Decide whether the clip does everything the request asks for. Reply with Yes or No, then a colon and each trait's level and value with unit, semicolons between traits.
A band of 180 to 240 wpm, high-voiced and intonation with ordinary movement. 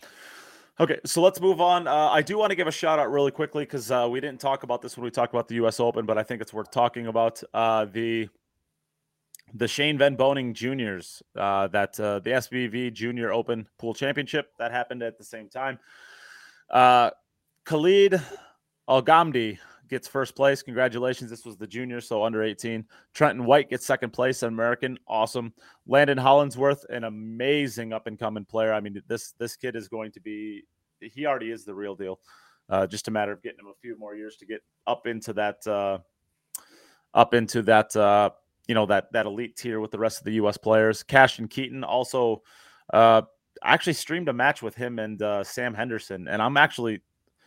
No: average, 195 wpm; low, 120 Hz; average, 3.3 semitones